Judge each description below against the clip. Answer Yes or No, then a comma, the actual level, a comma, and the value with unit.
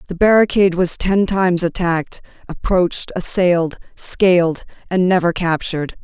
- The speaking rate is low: Yes, slow, 120 wpm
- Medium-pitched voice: Yes, medium, 180 Hz